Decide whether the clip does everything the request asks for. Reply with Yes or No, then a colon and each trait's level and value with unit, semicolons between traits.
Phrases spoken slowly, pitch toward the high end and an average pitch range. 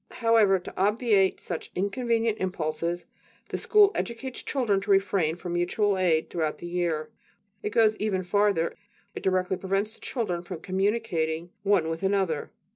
No: average, 145 wpm; high, 195 Hz; average, 3.4 semitones